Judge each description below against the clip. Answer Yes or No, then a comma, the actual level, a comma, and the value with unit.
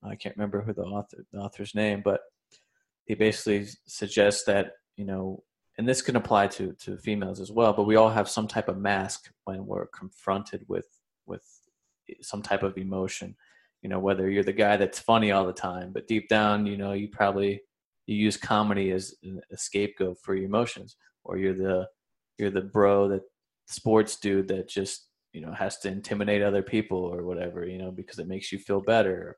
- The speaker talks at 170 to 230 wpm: Yes, average, 200 wpm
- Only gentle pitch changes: Yes, narrow, 1.6 semitones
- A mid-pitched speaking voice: No, low, 100 Hz